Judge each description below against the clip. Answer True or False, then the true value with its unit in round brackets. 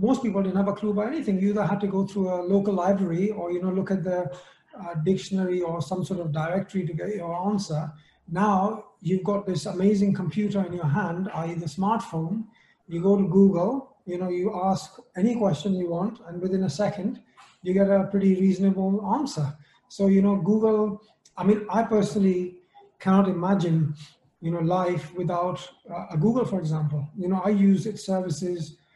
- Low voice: False (190 Hz)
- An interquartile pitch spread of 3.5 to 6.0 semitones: False (2.5 semitones)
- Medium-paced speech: True (195 wpm)